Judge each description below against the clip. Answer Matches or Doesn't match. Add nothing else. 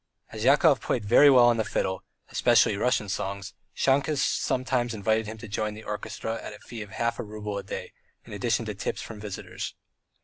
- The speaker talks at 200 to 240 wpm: Matches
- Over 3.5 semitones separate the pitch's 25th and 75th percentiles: Doesn't match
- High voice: Doesn't match